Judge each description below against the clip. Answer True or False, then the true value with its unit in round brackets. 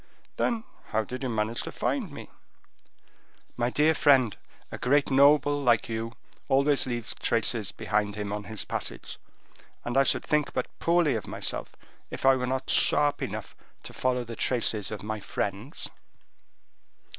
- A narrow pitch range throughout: False (4.2 semitones)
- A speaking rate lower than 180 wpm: True (155 wpm)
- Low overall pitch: True (125 Hz)